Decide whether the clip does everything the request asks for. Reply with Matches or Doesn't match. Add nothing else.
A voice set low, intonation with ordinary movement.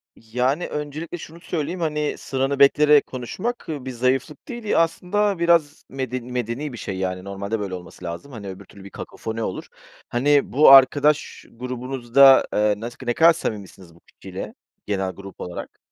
Doesn't match